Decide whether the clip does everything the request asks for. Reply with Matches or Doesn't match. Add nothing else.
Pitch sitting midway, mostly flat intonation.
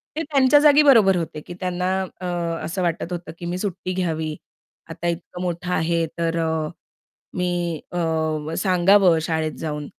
Matches